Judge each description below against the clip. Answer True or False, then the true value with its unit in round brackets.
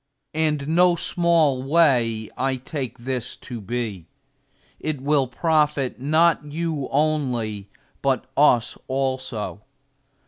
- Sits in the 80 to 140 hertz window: True (135 Hz)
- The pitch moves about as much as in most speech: True (4.0 semitones)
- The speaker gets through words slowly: True (105 wpm)